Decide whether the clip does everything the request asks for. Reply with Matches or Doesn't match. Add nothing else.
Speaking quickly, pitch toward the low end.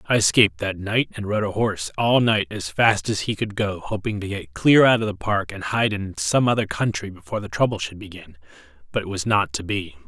Matches